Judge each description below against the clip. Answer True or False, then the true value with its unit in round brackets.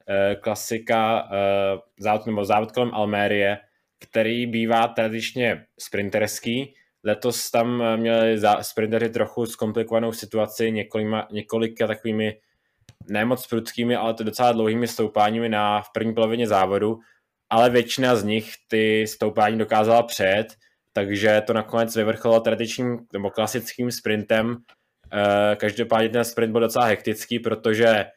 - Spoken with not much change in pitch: True (1.6 semitones)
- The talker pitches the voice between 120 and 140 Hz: False (110 Hz)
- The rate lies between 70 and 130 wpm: True (115 wpm)